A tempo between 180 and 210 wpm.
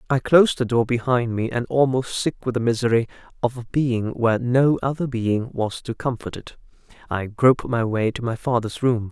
Yes: fast, 205 wpm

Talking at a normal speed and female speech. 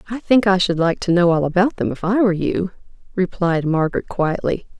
No: fast, 215 wpm; female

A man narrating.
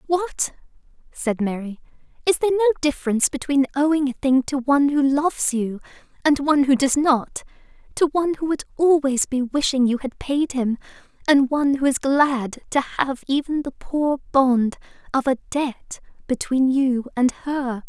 No: female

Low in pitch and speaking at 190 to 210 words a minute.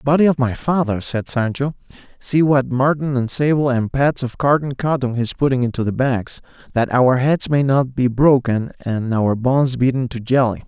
Yes: low, 130 Hz; average, 195 wpm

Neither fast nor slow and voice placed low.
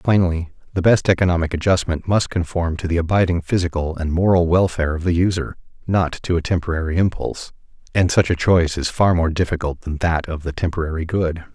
Yes: average, 185 wpm; very low, 85 Hz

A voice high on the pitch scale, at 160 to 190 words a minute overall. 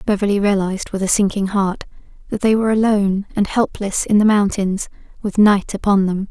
Yes: high, 200 Hz; average, 180 wpm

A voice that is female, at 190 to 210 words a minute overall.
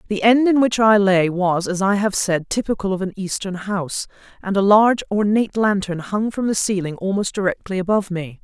Yes: female; fast, 205 wpm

